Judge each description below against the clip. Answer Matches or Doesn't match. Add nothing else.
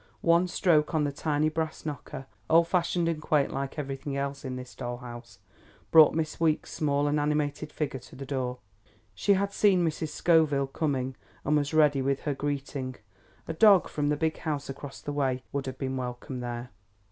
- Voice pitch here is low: Doesn't match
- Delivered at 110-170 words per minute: Doesn't match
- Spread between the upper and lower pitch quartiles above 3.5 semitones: Doesn't match